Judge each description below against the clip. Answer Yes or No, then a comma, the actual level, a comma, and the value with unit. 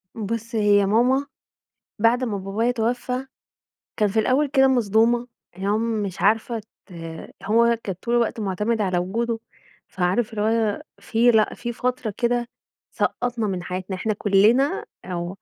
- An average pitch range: Yes, average, 3.0 semitones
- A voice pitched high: Yes, high, 225 Hz